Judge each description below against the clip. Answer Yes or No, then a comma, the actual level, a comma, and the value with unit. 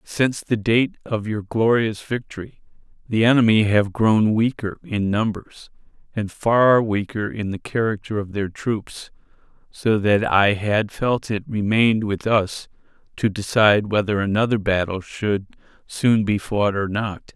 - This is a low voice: Yes, low, 105 Hz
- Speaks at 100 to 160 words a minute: Yes, average, 150 wpm